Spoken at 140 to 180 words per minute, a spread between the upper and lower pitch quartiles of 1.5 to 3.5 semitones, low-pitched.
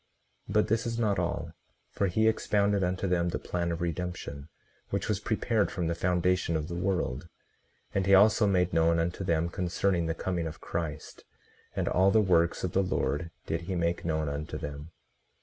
No: average, 190 wpm; average, 2.8 semitones; very low, 90 Hz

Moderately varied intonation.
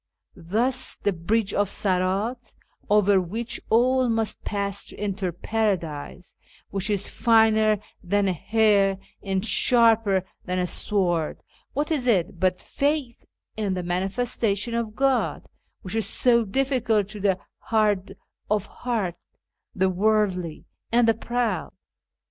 Yes: average, 3.4 semitones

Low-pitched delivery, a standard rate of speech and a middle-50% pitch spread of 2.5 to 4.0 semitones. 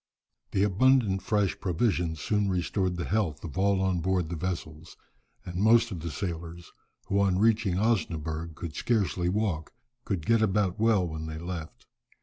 Yes: very low, 90 Hz; average, 160 wpm; average, 3.6 semitones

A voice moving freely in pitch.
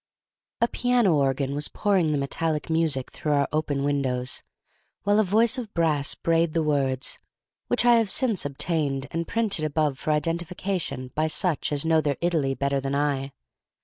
No: average, 3.8 semitones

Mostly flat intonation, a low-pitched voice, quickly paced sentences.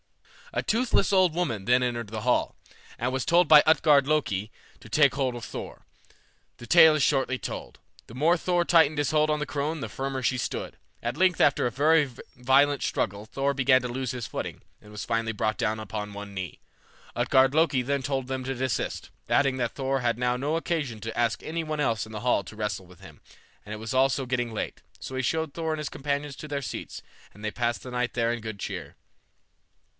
No: average, 4.2 semitones; low, 130 Hz; fast, 220 wpm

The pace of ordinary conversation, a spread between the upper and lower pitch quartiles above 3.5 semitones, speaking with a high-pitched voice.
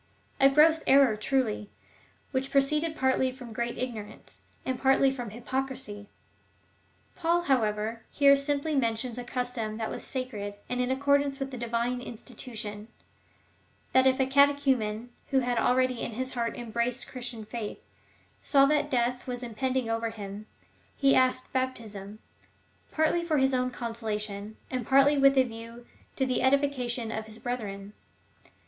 No: average, 160 wpm; average, 3.0 semitones; very high, 250 Hz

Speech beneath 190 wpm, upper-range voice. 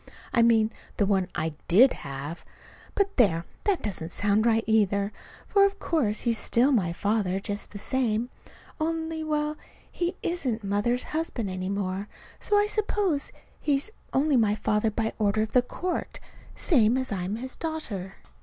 Yes: average, 160 wpm; high, 225 Hz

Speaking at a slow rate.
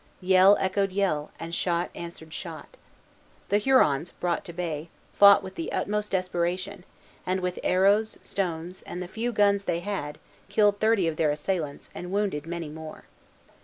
No: average, 160 wpm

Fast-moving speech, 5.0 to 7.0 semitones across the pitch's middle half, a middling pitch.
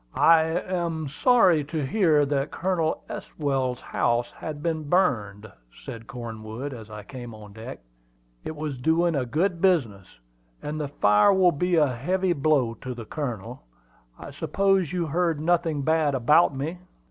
No: average, 155 wpm; wide, 5.4 semitones; medium, 150 Hz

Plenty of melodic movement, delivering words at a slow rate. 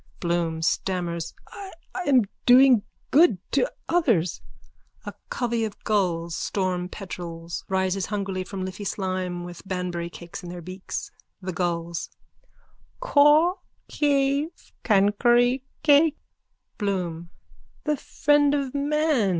Yes: wide, 7.6 semitones; slow, 110 wpm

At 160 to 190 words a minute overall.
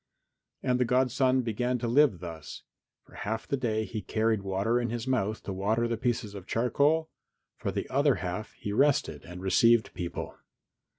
Yes: average, 175 wpm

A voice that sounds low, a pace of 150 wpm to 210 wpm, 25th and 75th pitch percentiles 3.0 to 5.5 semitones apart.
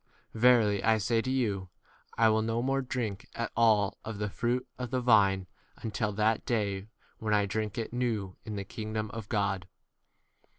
No: low, 110 Hz; average, 185 wpm; narrow, 2.5 semitones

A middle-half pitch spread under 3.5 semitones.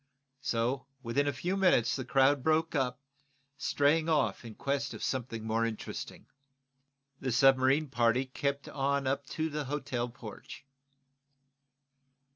Yes: average, 2.7 semitones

